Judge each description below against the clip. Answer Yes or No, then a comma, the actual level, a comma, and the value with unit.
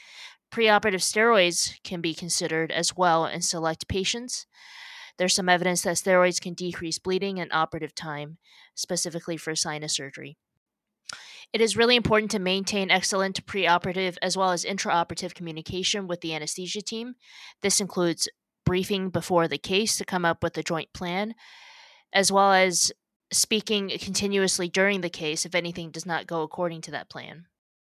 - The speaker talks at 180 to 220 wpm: No, average, 155 wpm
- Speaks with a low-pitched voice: No, medium, 180 Hz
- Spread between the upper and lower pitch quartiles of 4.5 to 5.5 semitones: No, average, 2.9 semitones